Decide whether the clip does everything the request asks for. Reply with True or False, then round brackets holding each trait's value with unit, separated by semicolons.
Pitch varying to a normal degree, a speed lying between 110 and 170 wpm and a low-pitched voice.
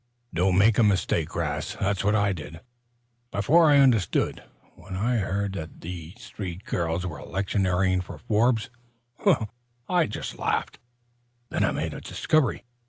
True (3.7 semitones; 140 wpm; 95 Hz)